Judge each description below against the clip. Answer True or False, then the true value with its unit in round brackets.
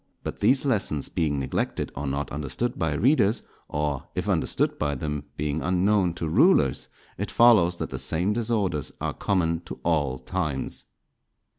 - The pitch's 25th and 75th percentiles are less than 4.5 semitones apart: False (5.5 semitones)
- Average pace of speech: True (155 wpm)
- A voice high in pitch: False (80 Hz)